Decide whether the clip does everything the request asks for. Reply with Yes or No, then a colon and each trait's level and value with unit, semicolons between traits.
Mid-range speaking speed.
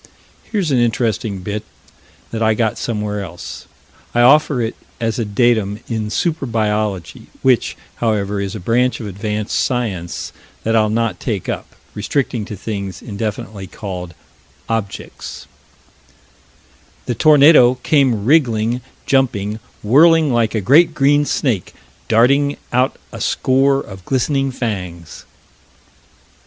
No: slow, 125 wpm